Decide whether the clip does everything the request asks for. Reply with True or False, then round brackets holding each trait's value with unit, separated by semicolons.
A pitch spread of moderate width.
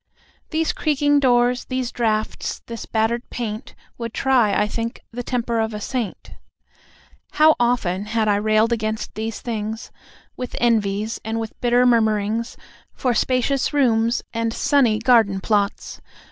False (2.3 semitones)